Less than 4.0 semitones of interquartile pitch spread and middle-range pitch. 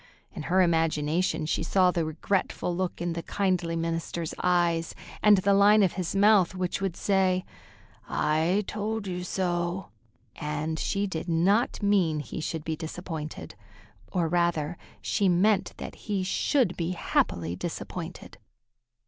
Yes: average, 2.8 semitones; medium, 175 Hz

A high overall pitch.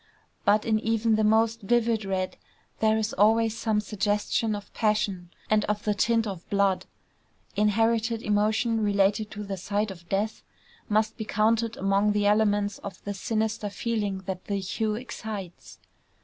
Yes: high, 210 Hz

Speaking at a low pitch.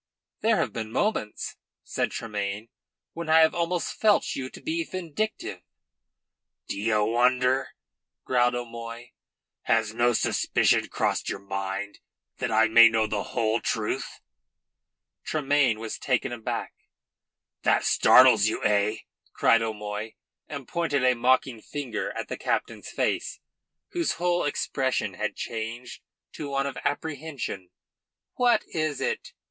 Yes: low, 120 Hz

